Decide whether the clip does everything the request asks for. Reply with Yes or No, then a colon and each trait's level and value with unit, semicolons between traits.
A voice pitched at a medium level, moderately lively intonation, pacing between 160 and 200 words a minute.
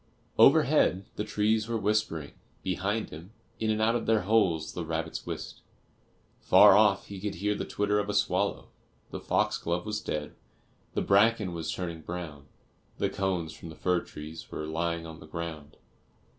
No: very low, 90 Hz; average, 4.3 semitones; average, 170 wpm